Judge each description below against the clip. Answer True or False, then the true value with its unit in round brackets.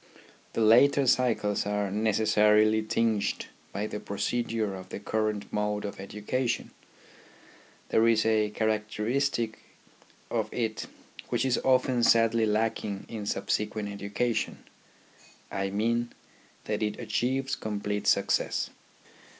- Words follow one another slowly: True (115 wpm)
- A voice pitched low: True (110 Hz)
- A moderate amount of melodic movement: False (1.8 semitones)